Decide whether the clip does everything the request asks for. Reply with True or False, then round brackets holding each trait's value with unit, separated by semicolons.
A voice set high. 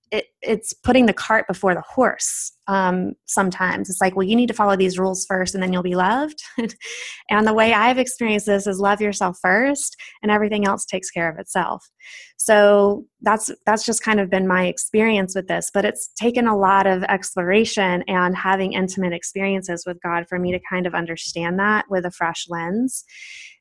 True (200 Hz)